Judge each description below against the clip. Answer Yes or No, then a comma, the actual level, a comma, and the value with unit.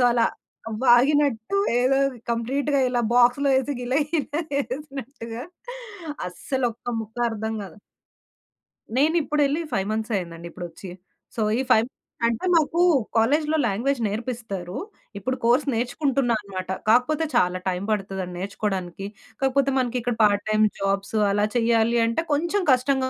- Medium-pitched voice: No, high, 240 Hz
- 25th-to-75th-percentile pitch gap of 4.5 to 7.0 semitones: Yes, average, 4.9 semitones